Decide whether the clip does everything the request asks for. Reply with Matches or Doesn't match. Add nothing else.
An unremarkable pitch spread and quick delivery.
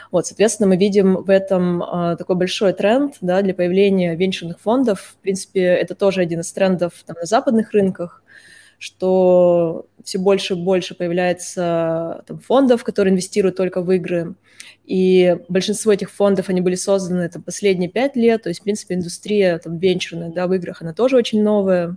Doesn't match